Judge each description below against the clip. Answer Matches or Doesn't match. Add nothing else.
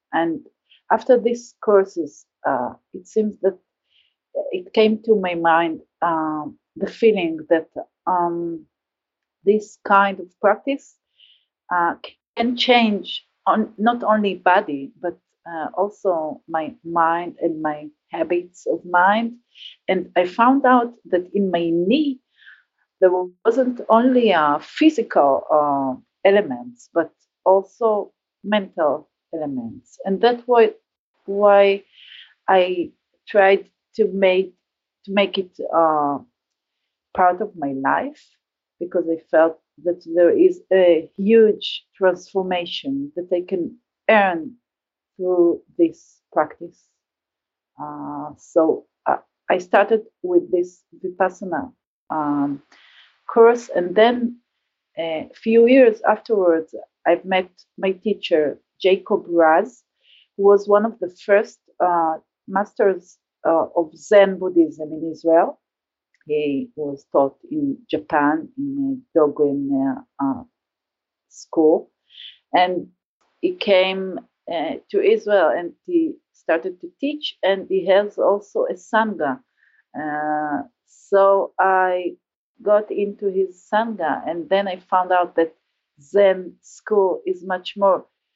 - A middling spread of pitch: Matches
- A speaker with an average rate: Doesn't match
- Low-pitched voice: Doesn't match